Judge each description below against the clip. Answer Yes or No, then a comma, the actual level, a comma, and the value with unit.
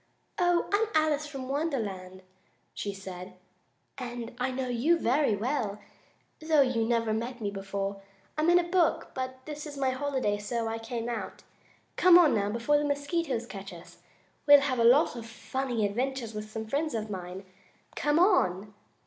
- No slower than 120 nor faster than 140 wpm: No, average, 170 wpm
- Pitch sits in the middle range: No, high, 245 Hz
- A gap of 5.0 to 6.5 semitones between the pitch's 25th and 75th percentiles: Yes, wide, 5.5 semitones